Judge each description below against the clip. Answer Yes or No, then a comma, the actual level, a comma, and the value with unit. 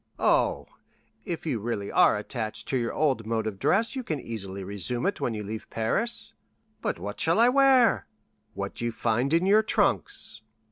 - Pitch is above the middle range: No, low, 120 Hz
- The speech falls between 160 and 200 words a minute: Yes, average, 180 wpm